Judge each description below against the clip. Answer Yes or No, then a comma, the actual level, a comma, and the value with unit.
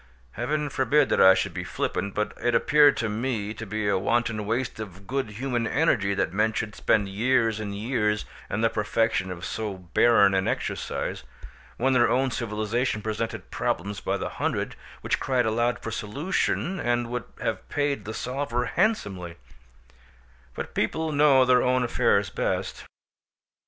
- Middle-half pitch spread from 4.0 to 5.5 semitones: No, average, 3.6 semitones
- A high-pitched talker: No, low, 115 Hz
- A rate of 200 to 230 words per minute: No, average, 160 wpm